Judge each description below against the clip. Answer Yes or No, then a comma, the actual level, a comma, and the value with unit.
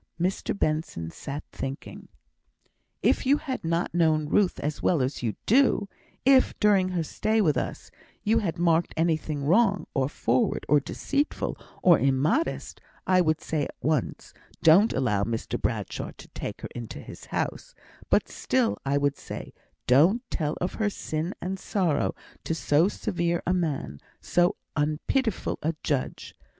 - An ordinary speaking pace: Yes, average, 155 wpm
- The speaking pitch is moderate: Yes, medium, 165 Hz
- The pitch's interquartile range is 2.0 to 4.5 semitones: No, average, 5.1 semitones